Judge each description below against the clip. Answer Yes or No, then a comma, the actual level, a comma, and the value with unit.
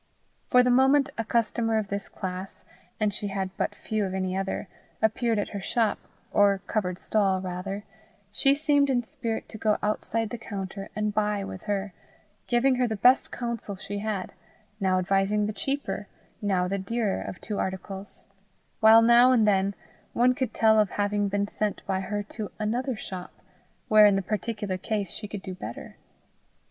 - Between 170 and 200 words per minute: Yes, average, 175 wpm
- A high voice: Yes, high, 210 Hz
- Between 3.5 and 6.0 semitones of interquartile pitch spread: No, average, 2.7 semitones